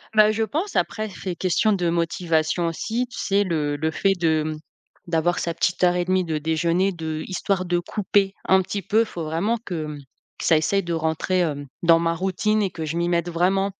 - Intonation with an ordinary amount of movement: Yes, average, 3.2 semitones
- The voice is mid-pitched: Yes, medium, 175 Hz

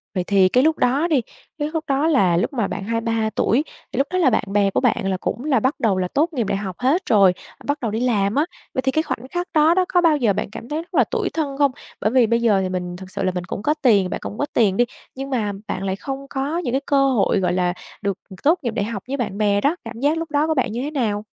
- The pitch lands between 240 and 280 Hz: Yes, high, 245 Hz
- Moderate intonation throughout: No, wide, 6.3 semitones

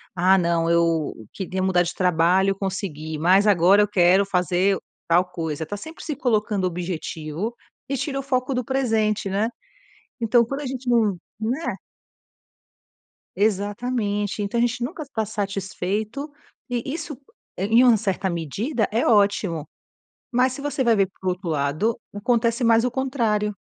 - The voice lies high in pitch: Yes, high, 205 Hz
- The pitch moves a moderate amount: Yes, average, 4.9 semitones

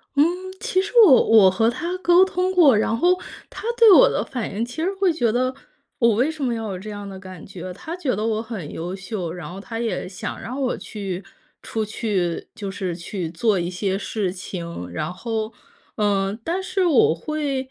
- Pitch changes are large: Yes, wide, 6.8 semitones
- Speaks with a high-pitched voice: Yes, high, 220 Hz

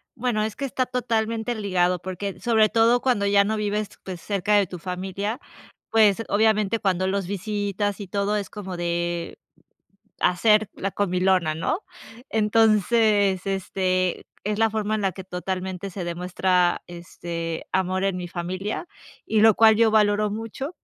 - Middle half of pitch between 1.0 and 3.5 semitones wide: Yes, average, 2.9 semitones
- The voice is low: No, high, 200 Hz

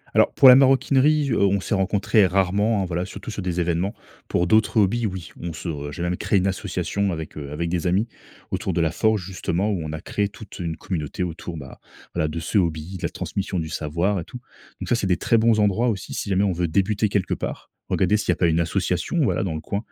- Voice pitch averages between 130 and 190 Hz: No, very low, 95 Hz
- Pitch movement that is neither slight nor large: Yes, average, 3.5 semitones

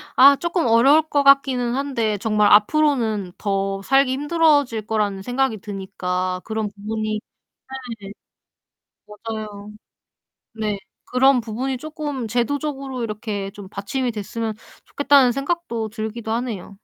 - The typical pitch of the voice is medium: No, high, 225 Hz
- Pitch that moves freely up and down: No, average, 4.5 semitones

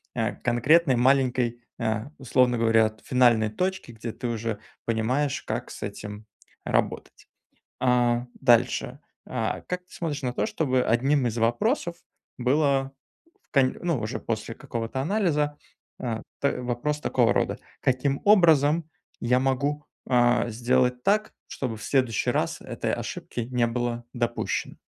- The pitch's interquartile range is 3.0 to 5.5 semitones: Yes, average, 3.3 semitones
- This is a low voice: Yes, low, 125 Hz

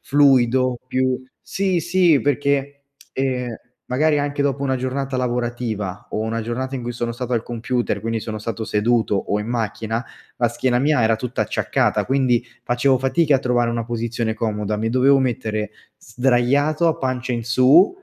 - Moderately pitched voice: No, low, 125 Hz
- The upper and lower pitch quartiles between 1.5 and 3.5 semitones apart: Yes, average, 2.8 semitones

